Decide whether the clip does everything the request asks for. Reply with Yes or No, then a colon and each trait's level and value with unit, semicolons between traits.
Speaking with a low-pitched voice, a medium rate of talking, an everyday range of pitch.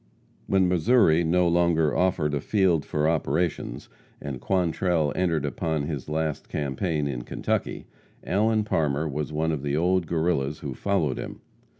Yes: very low, 80 Hz; average, 155 wpm; average, 3.3 semitones